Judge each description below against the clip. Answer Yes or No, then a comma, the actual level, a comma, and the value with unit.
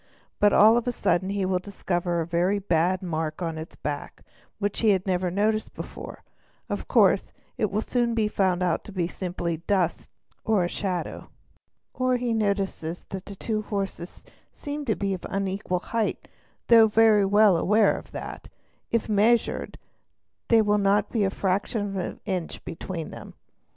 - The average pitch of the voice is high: Yes, high, 195 Hz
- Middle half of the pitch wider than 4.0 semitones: No, average, 3.1 semitones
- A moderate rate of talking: Yes, average, 170 wpm